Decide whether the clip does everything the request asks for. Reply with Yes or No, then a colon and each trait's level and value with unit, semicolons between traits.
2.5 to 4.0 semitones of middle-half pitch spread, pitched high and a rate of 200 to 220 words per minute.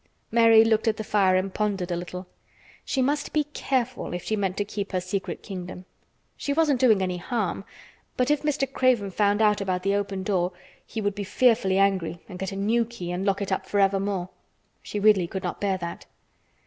Yes: average, 3.1 semitones; high, 200 Hz; fast, 205 wpm